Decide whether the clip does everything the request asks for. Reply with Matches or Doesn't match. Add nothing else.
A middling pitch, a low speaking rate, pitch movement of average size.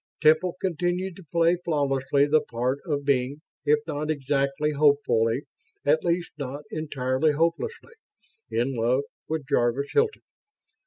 Matches